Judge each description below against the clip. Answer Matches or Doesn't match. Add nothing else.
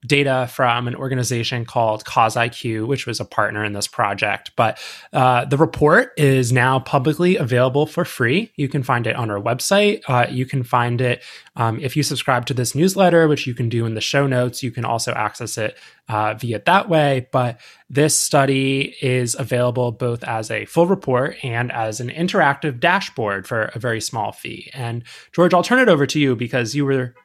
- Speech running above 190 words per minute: Matches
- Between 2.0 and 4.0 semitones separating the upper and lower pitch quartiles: Matches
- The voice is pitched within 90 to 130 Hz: Matches